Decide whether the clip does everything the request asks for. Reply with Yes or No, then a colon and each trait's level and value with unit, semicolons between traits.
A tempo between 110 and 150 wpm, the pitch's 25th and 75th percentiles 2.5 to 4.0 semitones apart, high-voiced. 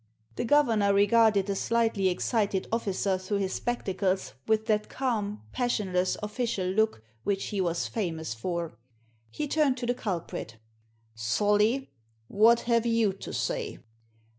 Yes: average, 140 wpm; average, 3.7 semitones; high, 205 Hz